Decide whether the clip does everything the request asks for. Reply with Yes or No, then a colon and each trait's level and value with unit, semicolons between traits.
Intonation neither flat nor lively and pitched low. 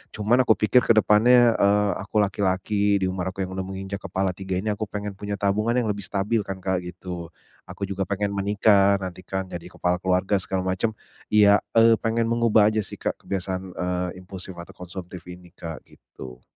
No: narrow, 2.2 semitones; low, 100 Hz